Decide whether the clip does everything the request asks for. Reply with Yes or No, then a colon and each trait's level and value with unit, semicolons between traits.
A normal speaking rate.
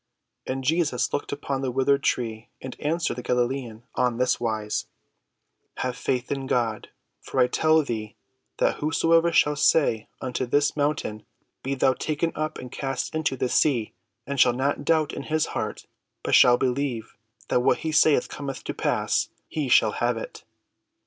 Yes: average, 170 wpm